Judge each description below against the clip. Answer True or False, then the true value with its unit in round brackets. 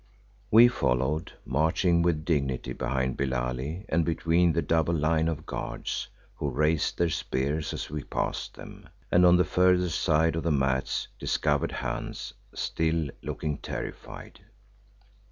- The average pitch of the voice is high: False (80 Hz)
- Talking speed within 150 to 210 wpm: False (135 wpm)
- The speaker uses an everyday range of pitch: True (3.4 semitones)